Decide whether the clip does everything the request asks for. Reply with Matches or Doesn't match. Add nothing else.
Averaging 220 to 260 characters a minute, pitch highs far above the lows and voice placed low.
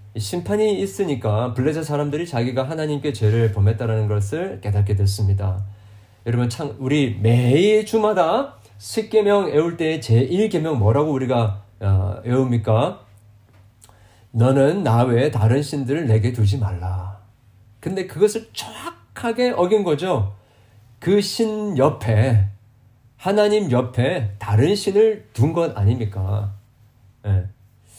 Matches